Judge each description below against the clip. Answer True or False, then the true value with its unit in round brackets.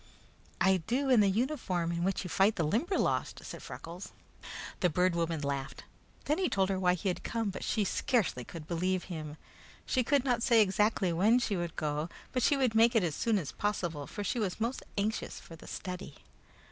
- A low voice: False (190 Hz)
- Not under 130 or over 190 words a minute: False (205 wpm)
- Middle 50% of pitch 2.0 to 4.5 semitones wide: False (5.0 semitones)